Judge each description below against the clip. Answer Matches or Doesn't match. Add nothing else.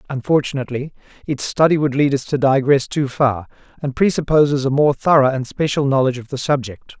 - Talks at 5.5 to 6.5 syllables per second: Matches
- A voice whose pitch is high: Doesn't match